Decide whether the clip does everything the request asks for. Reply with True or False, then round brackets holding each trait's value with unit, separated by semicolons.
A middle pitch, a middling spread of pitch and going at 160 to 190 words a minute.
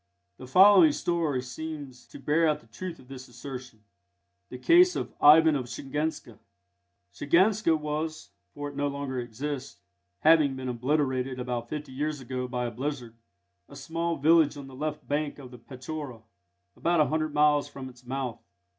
True (145 Hz; 3.5 semitones; 165 wpm)